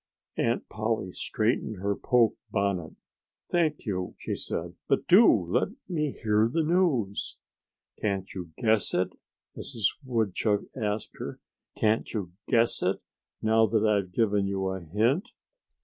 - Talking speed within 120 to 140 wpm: Yes, slow, 135 wpm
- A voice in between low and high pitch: No, low, 110 Hz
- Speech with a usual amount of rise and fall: Yes, average, 3.4 semitones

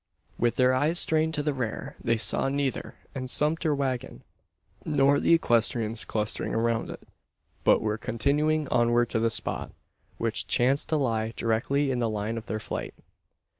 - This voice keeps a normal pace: Yes, average, 165 wpm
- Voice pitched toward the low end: Yes, low, 125 Hz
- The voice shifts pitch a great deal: No, average, 4.0 semitones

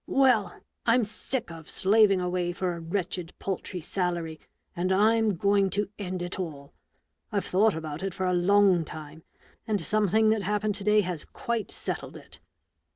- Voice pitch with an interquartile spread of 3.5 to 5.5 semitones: No, average, 3.1 semitones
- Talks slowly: No, average, 165 wpm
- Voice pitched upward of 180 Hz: Yes, high, 190 Hz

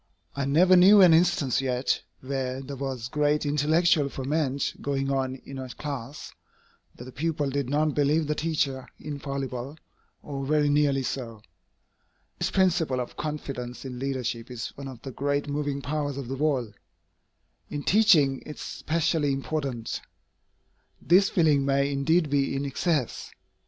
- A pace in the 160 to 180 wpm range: No, average, 150 wpm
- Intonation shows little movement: Yes, narrow, 2.3 semitones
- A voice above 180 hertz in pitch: No, medium, 140 Hz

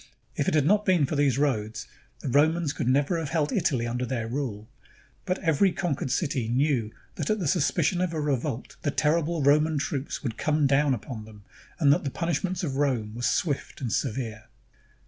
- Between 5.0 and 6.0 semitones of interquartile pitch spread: No, average, 4.1 semitones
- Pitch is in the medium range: Yes, medium, 145 Hz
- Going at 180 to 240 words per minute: Yes, average, 195 wpm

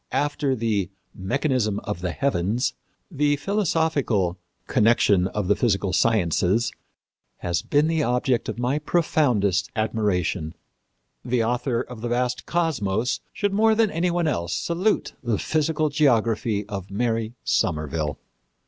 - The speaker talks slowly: Yes, slow, 130 wpm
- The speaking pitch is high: No, low, 120 Hz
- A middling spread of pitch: No, wide, 6.6 semitones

